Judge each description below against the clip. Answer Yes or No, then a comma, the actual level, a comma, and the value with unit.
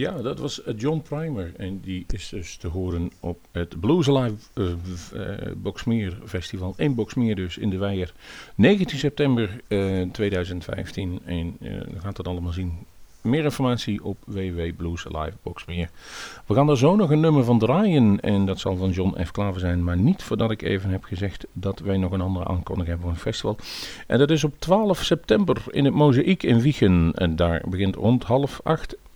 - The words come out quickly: No, average, 185 wpm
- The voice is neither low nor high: No, low, 100 Hz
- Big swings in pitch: Yes, wide, 5.7 semitones